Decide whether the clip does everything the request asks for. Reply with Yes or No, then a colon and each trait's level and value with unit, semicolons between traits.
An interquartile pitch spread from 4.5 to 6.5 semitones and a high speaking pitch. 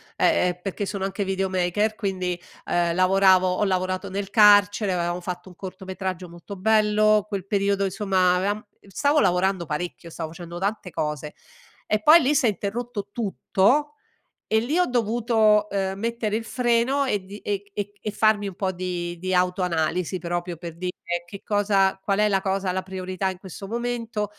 No: narrow, 2.6 semitones; high, 195 Hz